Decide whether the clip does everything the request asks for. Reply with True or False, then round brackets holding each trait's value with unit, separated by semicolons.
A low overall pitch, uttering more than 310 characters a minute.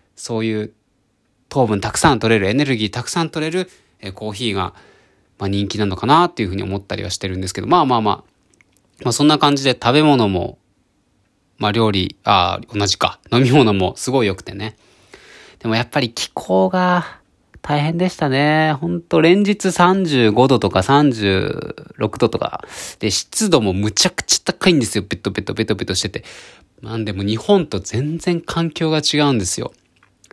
True (115 Hz; 340 characters per minute)